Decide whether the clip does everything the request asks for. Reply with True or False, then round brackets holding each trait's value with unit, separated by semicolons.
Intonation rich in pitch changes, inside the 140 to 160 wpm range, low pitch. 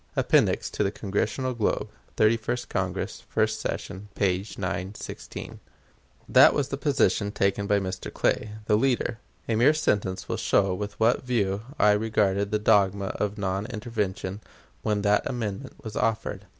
False (2.6 semitones; 150 wpm; 105 Hz)